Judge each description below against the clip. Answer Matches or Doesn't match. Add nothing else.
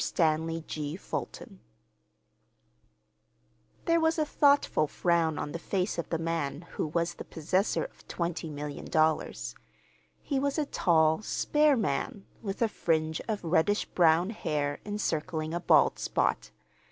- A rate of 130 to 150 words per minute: Matches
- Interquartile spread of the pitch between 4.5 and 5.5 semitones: Matches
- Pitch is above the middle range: Doesn't match